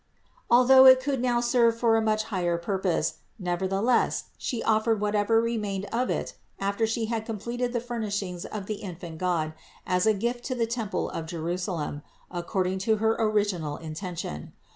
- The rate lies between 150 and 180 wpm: Yes, average, 170 wpm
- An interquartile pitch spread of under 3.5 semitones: No, average, 4.3 semitones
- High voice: Yes, high, 210 Hz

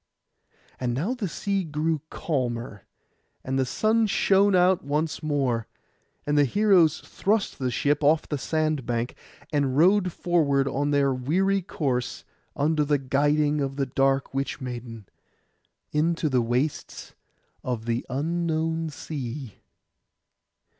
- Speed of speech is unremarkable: No, slow, 130 wpm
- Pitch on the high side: No, medium, 145 Hz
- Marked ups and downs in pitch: No, average, 3.9 semitones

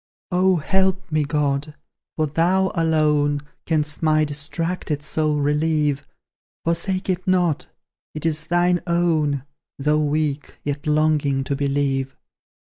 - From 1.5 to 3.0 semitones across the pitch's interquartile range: Yes, narrow, 2.6 semitones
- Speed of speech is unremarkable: No, slow, 120 wpm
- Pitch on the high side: No, medium, 155 Hz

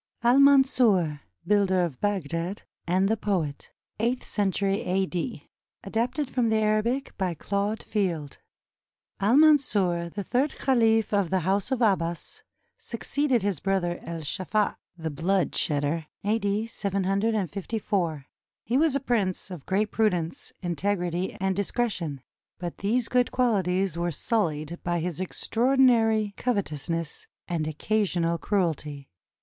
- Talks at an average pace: No, slow, 125 wpm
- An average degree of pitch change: Yes, average, 4.5 semitones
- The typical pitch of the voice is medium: No, high, 195 Hz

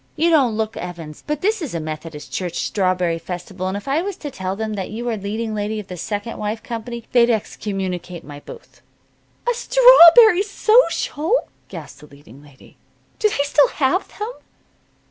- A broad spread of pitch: Yes, wide, 8.9 semitones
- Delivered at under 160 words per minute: No, average, 180 wpm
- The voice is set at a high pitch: Yes, high, 215 Hz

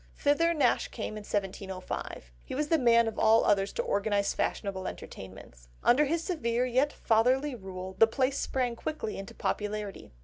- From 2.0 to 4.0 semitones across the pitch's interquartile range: No, average, 5.0 semitones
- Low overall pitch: No, high, 225 Hz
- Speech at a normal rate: Yes, average, 165 wpm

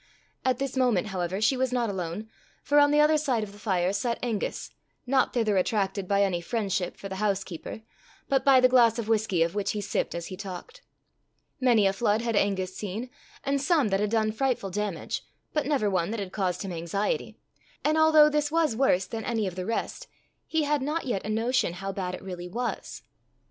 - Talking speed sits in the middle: No, fast, 210 wpm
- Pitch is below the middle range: No, high, 215 Hz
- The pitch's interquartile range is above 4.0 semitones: Yes, average, 5.1 semitones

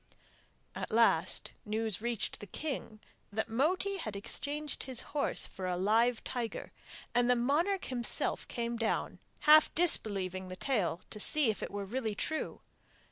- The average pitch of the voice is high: Yes, high, 235 Hz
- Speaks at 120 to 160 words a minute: Yes, average, 150 wpm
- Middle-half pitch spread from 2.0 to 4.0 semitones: No, average, 5.3 semitones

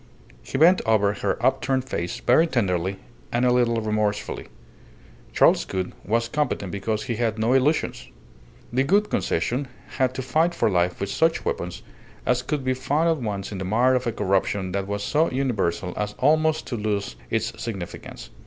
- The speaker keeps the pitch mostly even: No, average, 4.8 semitones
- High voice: No, low, 115 Hz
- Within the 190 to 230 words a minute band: No, average, 175 wpm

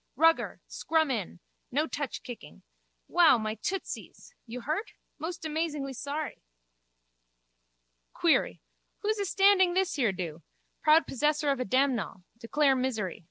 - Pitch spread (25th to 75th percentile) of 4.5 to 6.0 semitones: Yes, average, 5.1 semitones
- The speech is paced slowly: Yes, slow, 115 wpm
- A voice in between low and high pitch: No, very high, 290 Hz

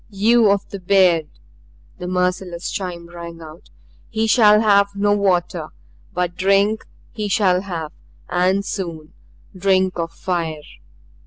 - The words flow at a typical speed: No, slow, 130 wpm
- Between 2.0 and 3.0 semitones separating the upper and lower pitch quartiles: Yes, narrow, 2.5 semitones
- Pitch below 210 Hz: Yes, medium, 185 Hz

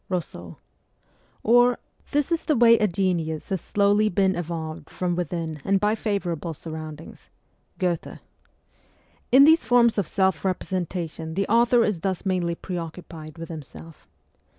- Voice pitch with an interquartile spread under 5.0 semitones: Yes, average, 4.2 semitones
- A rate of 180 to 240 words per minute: No, average, 150 wpm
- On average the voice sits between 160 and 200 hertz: Yes, medium, 185 Hz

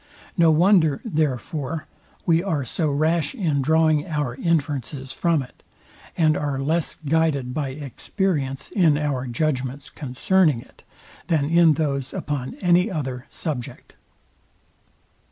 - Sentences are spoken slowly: Yes, slow, 120 wpm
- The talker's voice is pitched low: No, medium, 150 Hz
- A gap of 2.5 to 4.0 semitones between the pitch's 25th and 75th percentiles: Yes, average, 3.3 semitones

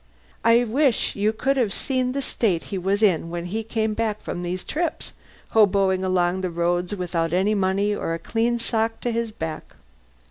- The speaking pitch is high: Yes, high, 205 Hz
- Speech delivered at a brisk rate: No, average, 190 wpm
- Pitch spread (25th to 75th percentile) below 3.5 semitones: No, average, 4.1 semitones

